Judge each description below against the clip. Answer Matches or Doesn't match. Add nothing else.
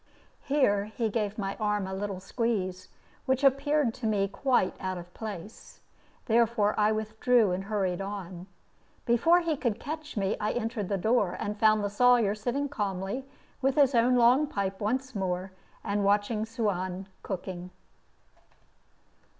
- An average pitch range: Matches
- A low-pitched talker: Doesn't match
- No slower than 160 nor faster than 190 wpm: Doesn't match